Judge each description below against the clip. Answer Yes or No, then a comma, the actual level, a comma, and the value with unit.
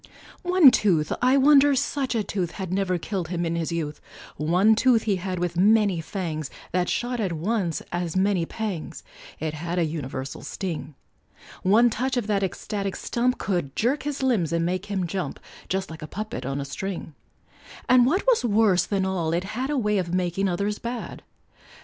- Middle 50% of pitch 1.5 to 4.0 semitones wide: No, average, 5.0 semitones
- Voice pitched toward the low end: No, high, 190 Hz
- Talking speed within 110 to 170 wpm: No, average, 185 wpm